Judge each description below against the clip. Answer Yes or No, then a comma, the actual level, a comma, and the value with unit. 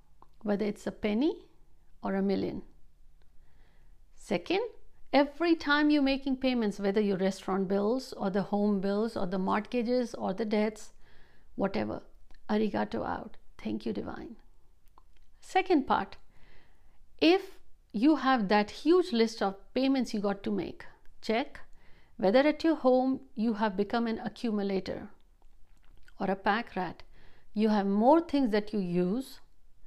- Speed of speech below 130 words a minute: No, average, 135 wpm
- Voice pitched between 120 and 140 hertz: No, high, 220 Hz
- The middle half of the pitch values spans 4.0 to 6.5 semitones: Yes, average, 5.0 semitones